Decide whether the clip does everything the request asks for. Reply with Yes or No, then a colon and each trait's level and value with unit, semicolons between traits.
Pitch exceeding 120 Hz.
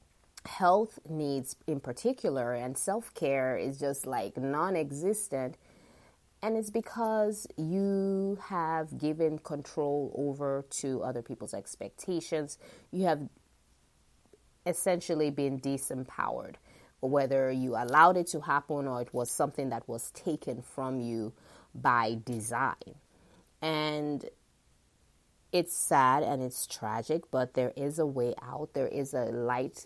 Yes: medium, 140 Hz